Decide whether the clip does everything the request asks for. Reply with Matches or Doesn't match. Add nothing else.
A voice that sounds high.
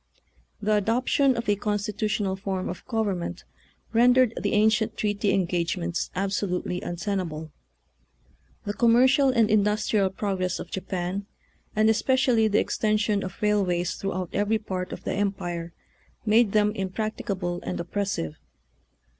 Matches